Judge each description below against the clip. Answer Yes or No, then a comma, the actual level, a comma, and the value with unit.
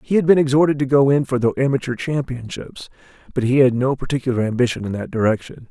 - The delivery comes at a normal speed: No, fast, 210 wpm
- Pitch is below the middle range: Yes, low, 130 Hz